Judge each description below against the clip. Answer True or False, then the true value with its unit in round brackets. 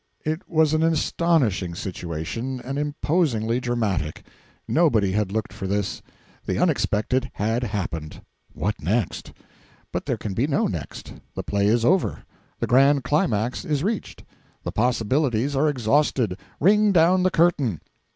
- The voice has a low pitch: True (125 Hz)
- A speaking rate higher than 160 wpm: False (140 wpm)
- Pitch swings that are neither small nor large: False (6.6 semitones)